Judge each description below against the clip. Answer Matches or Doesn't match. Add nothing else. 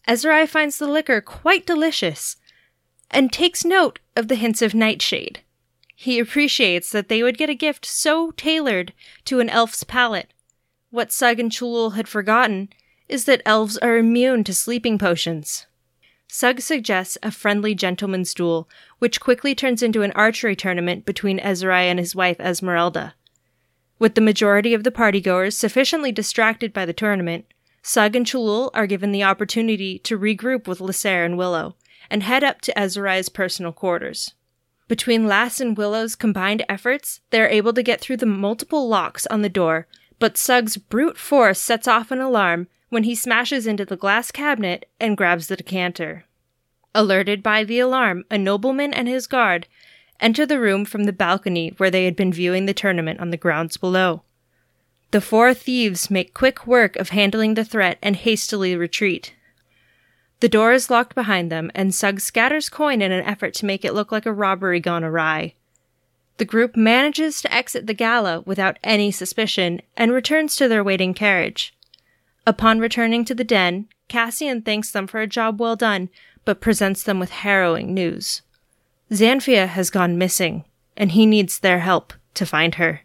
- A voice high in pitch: Matches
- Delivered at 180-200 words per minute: Doesn't match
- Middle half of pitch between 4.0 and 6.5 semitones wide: Matches